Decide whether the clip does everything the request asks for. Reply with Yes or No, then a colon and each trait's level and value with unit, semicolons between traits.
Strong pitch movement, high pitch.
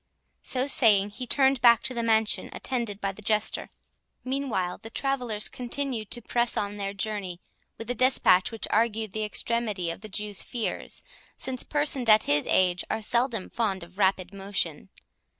No: average, 3.6 semitones; high, 220 Hz